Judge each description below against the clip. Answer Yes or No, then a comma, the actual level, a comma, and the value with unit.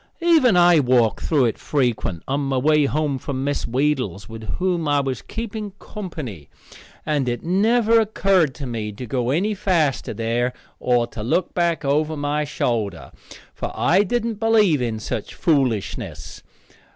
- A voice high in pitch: No, medium, 145 Hz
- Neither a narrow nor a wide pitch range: No, wide, 6.8 semitones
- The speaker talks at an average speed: Yes, average, 155 wpm